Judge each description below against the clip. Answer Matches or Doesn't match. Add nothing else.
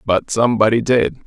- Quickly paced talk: Doesn't match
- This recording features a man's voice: Matches